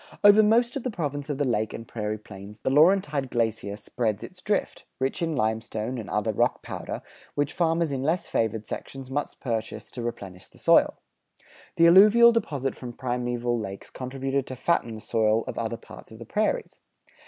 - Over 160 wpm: Yes, average, 185 wpm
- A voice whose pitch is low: Yes, low, 130 Hz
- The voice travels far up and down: Yes, wide, 6.4 semitones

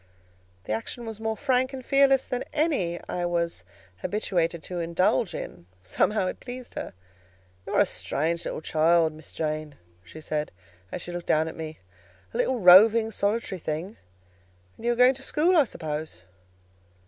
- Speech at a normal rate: Yes, average, 165 wpm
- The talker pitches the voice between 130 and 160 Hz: No, medium, 180 Hz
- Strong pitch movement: Yes, wide, 7.2 semitones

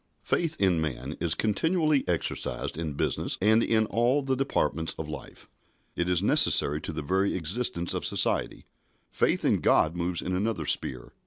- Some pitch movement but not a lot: No, wide, 6.5 semitones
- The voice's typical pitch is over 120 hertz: No, very low, 90 Hz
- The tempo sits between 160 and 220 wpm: Yes, average, 165 wpm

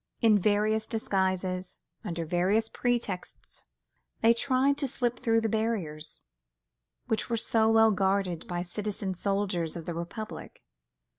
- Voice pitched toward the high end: Yes, high, 205 Hz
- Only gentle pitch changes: No, average, 3.6 semitones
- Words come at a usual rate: No, slow, 130 wpm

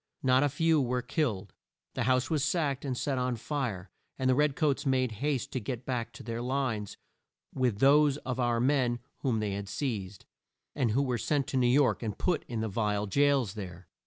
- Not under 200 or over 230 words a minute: Yes, fast, 205 wpm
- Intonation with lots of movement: No, average, 3.8 semitones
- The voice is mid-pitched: No, low, 130 Hz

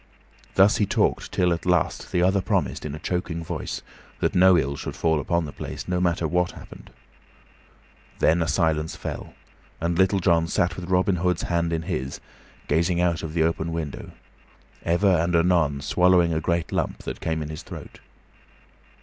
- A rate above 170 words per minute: Yes, average, 180 wpm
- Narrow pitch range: Yes, narrow, 1.9 semitones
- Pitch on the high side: No, very low, 85 Hz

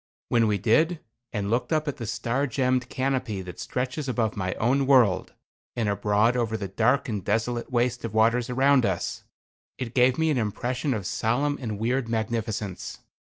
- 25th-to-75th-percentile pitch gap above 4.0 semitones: No, average, 2.8 semitones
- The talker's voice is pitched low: Yes, low, 120 Hz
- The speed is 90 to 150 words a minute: No, average, 175 wpm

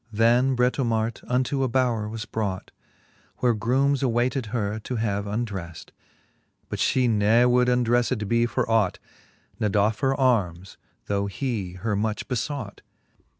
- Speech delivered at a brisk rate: No, average, 140 wpm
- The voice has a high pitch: No, low, 115 Hz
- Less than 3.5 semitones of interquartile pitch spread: Yes, average, 3.1 semitones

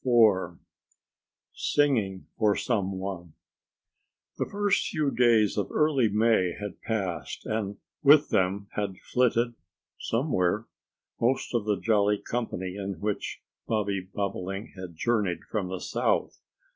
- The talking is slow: Yes, slow, 120 wpm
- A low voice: Yes, low, 105 Hz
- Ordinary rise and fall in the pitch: Yes, average, 3.7 semitones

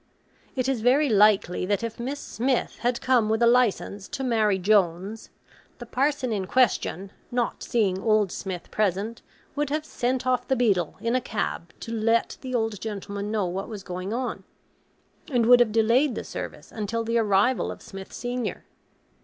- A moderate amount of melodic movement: Yes, average, 3.7 semitones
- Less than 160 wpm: No, average, 175 wpm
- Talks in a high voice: Yes, high, 225 Hz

